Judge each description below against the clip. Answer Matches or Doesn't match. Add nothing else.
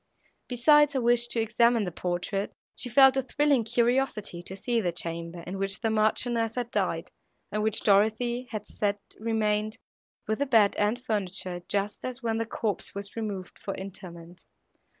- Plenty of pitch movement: Doesn't match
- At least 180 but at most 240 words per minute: Doesn't match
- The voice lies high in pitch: Matches